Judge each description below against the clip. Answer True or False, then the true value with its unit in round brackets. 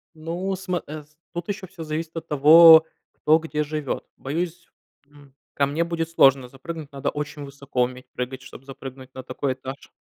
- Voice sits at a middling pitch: True (150 Hz)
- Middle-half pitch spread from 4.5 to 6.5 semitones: False (3.3 semitones)